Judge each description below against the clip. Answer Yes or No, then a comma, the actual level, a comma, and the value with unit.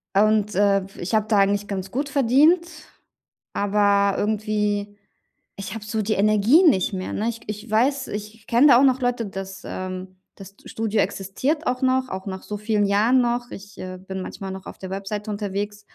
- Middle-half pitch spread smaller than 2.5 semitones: No, average, 2.9 semitones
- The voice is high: Yes, high, 210 Hz